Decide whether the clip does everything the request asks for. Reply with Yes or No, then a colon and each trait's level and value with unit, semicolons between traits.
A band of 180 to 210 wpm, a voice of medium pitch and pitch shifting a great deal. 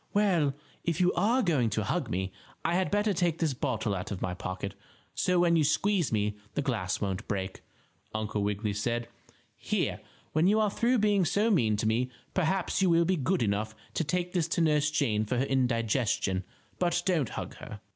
Yes: average, 195 wpm; medium, 145 Hz; wide, 8.8 semitones